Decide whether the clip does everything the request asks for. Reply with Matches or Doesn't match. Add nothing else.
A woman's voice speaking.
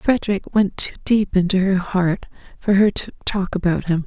Matches